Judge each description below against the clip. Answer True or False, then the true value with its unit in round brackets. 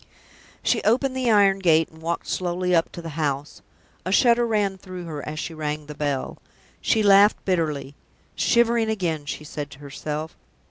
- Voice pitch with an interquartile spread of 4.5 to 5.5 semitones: True (5.2 semitones)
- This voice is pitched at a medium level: True (170 Hz)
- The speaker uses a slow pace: False (180 wpm)